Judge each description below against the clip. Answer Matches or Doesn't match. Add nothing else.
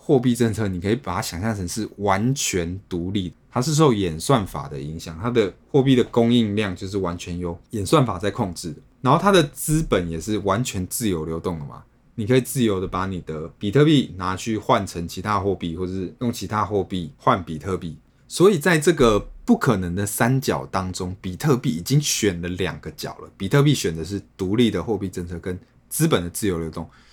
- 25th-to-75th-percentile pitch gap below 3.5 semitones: Doesn't match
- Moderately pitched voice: Doesn't match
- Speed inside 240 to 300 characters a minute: Doesn't match